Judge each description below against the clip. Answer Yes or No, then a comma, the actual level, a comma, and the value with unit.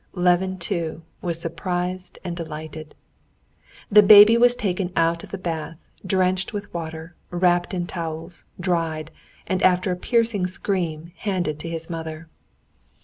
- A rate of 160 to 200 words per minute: No, average, 140 wpm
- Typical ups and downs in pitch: No, narrow, 2.2 semitones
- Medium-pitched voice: Yes, medium, 175 Hz